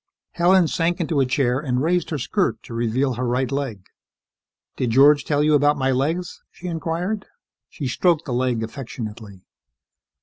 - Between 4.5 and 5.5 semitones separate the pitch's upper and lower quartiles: Yes, average, 4.9 semitones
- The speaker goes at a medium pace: Yes, average, 165 wpm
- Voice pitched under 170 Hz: Yes, medium, 140 Hz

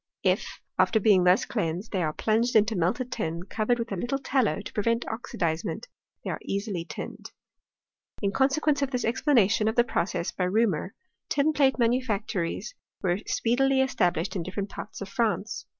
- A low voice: No, high, 215 Hz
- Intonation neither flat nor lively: Yes, average, 4.9 semitones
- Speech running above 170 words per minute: No, average, 165 wpm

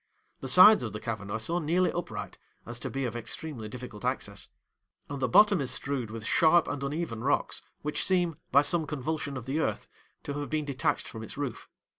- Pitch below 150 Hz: Yes, medium, 140 Hz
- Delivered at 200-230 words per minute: Yes, fast, 205 wpm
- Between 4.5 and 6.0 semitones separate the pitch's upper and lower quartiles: Yes, average, 4.9 semitones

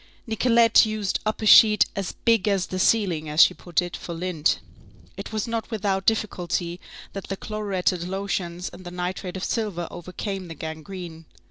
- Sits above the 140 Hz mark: Yes, high, 190 Hz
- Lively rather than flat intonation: No, average, 3.3 semitones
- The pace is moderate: Yes, average, 170 wpm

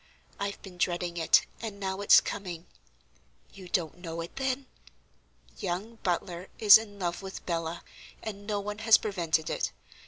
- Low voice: No, high, 190 Hz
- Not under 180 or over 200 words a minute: No, average, 155 wpm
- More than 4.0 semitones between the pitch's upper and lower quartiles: No, average, 3.1 semitones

